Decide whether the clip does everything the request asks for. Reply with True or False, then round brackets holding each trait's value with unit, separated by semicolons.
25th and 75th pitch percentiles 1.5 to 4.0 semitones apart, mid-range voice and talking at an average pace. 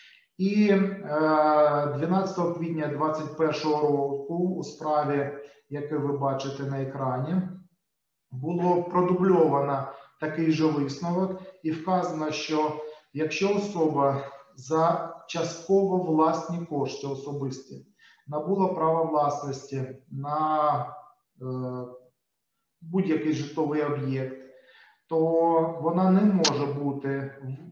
False (3.1 semitones; 155 Hz; 85 wpm)